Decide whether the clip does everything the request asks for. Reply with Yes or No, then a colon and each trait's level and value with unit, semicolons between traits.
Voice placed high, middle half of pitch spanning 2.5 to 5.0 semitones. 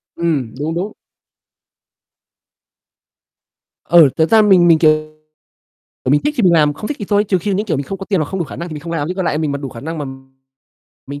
No: medium, 165 Hz; average, 4.1 semitones